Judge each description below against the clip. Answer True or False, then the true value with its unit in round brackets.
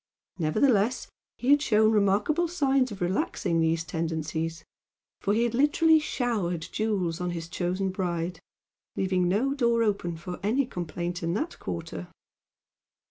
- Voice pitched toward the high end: True (195 Hz)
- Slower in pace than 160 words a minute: True (135 wpm)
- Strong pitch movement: True (5.7 semitones)